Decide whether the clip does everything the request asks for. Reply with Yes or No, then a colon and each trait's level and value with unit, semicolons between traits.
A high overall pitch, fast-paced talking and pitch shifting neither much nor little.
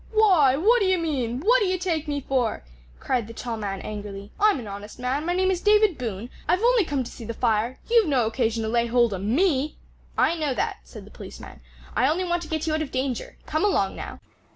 No: very high, 280 Hz; fast, 230 wpm; wide, 7.7 semitones